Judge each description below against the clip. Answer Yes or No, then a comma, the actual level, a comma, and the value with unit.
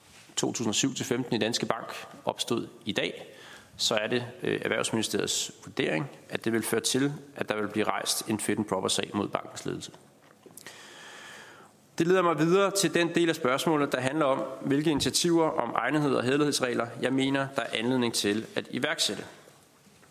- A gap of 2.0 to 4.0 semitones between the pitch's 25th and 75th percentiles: No, average, 4.9 semitones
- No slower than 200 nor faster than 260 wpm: No, average, 165 wpm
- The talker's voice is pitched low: Yes, low, 130 Hz